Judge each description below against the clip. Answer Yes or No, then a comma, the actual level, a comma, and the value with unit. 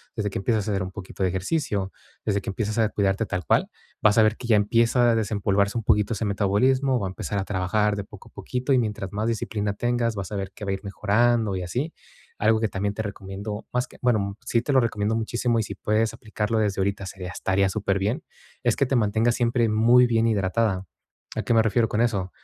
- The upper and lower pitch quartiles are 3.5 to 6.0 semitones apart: No, average, 2.8 semitones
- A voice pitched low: Yes, low, 105 Hz